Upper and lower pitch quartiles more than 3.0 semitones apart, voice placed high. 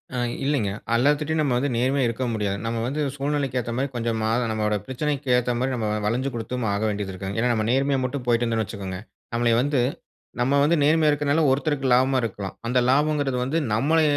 No: average, 3.7 semitones; low, 125 Hz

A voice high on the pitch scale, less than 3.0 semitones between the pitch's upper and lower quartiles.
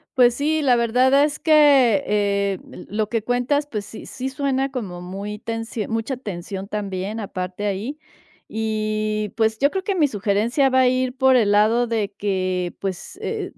No: high, 225 Hz; average, 4.4 semitones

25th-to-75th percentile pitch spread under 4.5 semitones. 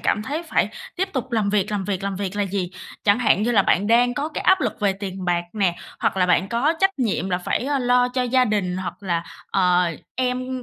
No: average, 4.9 semitones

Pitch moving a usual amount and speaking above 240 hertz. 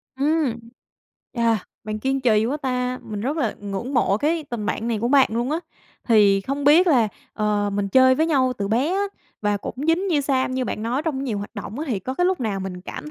Yes: average, 4.9 semitones; very high, 250 Hz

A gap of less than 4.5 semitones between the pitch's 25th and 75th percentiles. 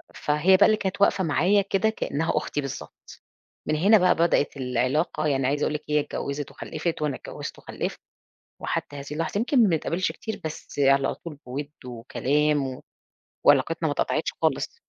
No: average, 5.0 semitones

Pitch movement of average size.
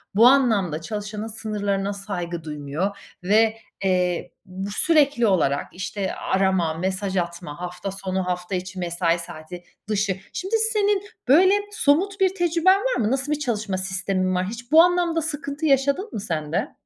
No: wide, 7.6 semitones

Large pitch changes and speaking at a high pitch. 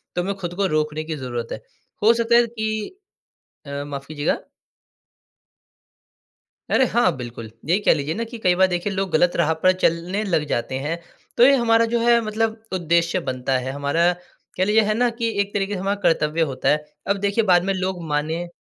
No: wide, 5.9 semitones; medium, 180 Hz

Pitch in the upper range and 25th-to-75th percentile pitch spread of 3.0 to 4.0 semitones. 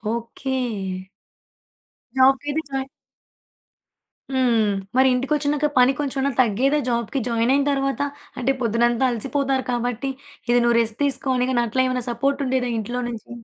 No: very high, 255 Hz; narrow, 2.4 semitones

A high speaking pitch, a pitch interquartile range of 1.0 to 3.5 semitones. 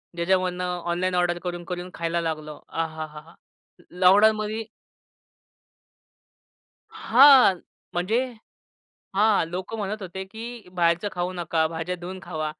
No: medium, 180 Hz; narrow, 2.5 semitones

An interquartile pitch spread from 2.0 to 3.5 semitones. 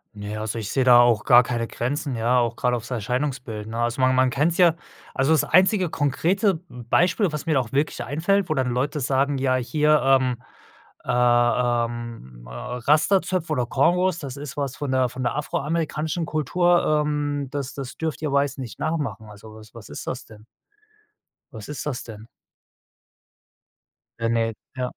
No: average, 4.1 semitones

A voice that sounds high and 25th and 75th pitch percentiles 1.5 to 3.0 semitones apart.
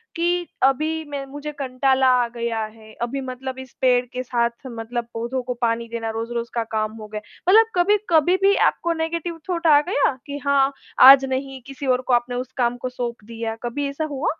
No: very high, 260 Hz; average, 3.5 semitones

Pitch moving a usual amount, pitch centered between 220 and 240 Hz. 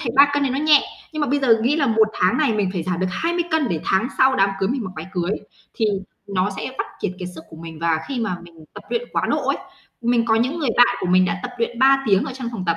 No: wide, 6.6 semitones; high, 230 Hz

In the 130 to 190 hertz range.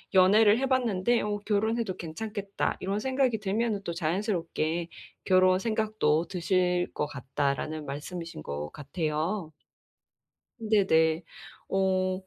Yes: medium, 185 Hz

